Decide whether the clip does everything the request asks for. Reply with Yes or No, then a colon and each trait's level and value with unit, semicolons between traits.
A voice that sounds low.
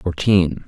Yes: very low, 90 Hz